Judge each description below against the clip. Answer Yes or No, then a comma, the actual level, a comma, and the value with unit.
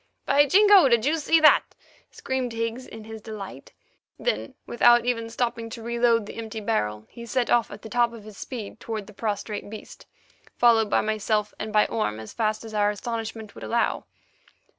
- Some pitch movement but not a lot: No, narrow, 1.9 semitones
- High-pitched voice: Yes, high, 225 Hz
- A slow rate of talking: No, average, 185 wpm